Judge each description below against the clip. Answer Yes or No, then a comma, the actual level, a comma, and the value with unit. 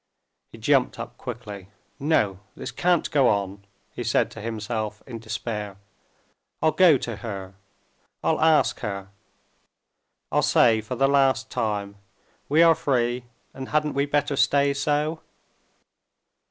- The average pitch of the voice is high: No, low, 120 Hz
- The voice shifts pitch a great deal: Yes, wide, 5.7 semitones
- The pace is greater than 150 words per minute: No, slow, 135 wpm